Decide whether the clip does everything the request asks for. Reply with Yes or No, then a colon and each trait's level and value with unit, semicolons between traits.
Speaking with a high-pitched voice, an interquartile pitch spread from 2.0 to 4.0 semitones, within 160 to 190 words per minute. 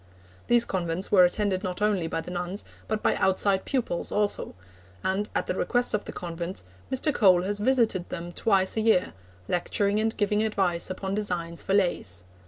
Yes: high, 195 Hz; average, 3.0 semitones; average, 180 wpm